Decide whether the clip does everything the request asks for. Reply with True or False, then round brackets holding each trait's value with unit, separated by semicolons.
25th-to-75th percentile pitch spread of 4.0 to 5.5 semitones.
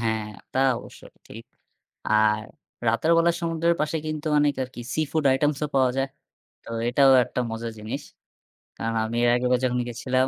True (4.4 semitones)